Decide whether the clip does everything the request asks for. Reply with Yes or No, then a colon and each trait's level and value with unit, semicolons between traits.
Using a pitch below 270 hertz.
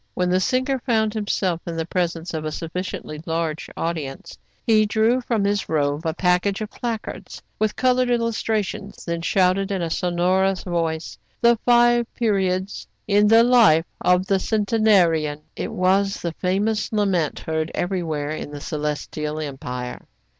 Yes: medium, 185 Hz